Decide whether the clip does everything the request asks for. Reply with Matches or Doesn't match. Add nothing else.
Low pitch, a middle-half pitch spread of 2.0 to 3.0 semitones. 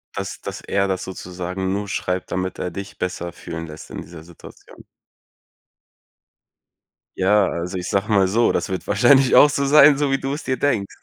Doesn't match